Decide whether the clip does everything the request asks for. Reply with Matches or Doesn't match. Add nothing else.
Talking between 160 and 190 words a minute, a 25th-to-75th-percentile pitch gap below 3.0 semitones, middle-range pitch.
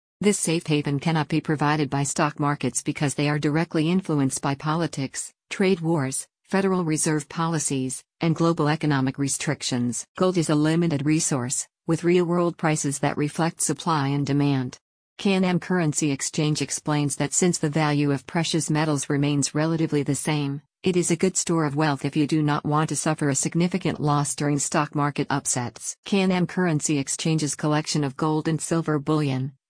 Matches